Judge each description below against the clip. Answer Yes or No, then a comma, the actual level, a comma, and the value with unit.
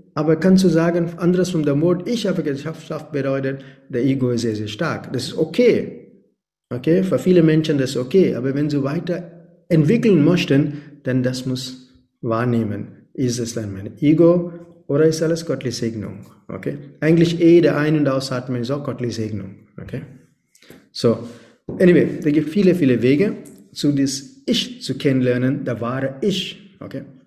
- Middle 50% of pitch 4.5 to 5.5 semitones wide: Yes, average, 5.0 semitones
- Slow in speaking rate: No, average, 165 wpm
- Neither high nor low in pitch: Yes, medium, 145 Hz